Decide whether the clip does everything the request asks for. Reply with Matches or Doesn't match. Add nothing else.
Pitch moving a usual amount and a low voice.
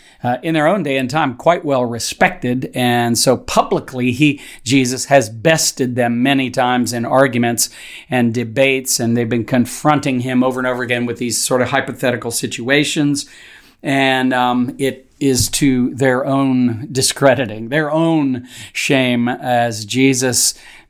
Doesn't match